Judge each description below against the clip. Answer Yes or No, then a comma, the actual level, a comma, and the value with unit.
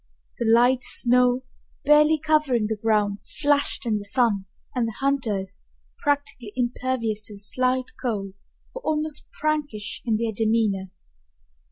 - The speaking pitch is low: No, high, 240 Hz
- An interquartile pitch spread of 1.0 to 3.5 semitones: No, average, 4.6 semitones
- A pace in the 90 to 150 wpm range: Yes, slow, 135 wpm